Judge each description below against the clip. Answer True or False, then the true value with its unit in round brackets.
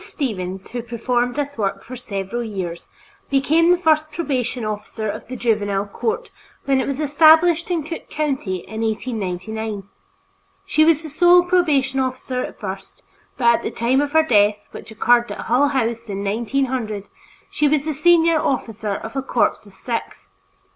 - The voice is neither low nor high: False (250 Hz)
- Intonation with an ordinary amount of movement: False (5.7 semitones)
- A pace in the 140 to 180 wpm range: True (170 wpm)